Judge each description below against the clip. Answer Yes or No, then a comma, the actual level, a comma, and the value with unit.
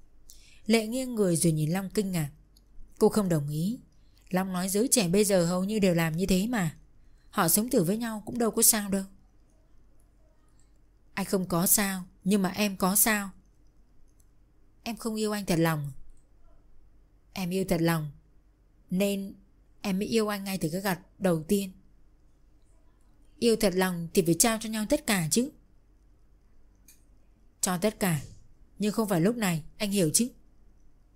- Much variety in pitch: Yes, wide, 6.9 semitones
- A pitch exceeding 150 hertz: Yes, medium, 185 Hz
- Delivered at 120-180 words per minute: Yes, average, 170 wpm